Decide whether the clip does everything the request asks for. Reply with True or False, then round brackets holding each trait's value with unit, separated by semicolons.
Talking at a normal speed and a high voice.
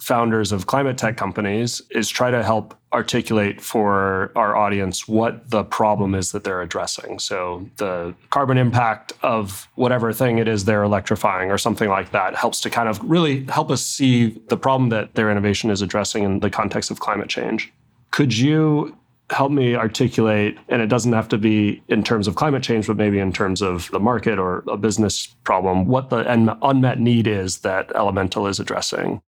False (190 wpm; 110 Hz)